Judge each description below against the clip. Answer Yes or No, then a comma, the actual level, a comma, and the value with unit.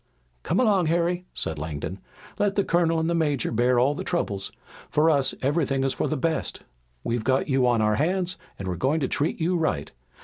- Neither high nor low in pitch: Yes, medium, 145 Hz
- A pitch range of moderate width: No, wide, 5.8 semitones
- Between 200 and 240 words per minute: Yes, fast, 205 wpm